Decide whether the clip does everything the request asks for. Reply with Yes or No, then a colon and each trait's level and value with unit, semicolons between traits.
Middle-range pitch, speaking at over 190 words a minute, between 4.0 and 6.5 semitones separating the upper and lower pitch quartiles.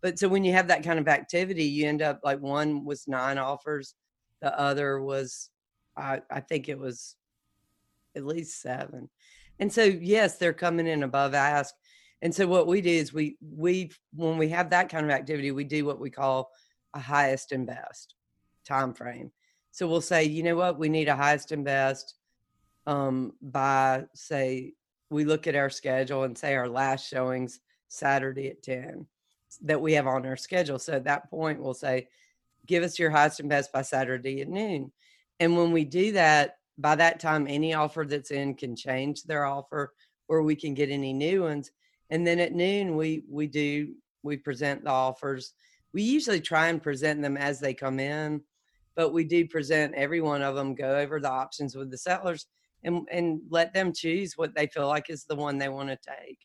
No: medium, 145 Hz; average, 200 wpm; average, 3.1 semitones